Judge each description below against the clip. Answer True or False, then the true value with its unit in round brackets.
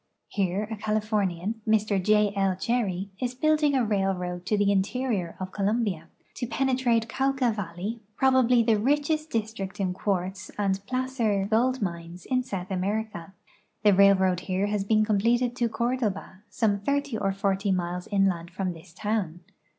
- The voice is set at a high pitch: True (205 Hz)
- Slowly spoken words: False (155 wpm)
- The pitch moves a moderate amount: True (3.7 semitones)